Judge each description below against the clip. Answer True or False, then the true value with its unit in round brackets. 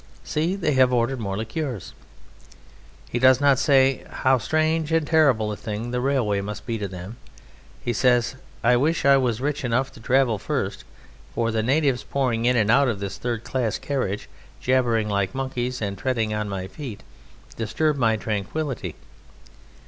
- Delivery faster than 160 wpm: True (170 wpm)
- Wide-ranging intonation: False (3.8 semitones)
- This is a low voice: True (125 Hz)